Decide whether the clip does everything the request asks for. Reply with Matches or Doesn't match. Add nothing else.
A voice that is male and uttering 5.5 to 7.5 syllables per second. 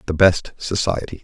Doesn't match